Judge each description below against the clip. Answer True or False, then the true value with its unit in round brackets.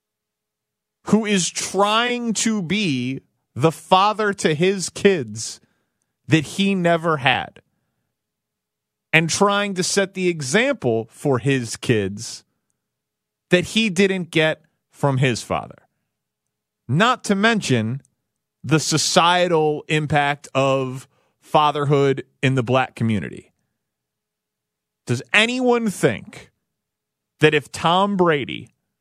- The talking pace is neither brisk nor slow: False (100 wpm)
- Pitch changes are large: True (6.9 semitones)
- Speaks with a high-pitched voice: False (155 Hz)